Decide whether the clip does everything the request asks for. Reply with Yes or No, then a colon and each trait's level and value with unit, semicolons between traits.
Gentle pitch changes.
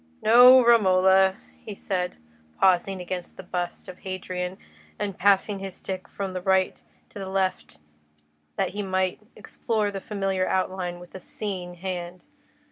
Yes: narrow, 1.3 semitones